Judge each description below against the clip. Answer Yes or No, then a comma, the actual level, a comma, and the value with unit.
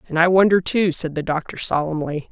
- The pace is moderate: No, fast, 210 wpm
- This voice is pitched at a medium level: Yes, medium, 165 Hz